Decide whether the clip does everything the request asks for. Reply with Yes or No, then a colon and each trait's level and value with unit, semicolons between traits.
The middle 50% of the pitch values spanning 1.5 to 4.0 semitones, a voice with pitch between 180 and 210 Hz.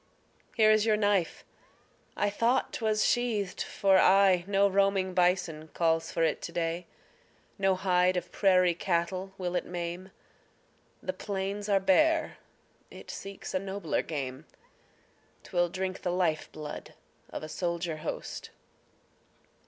Yes: narrow, 2.4 semitones; medium, 185 Hz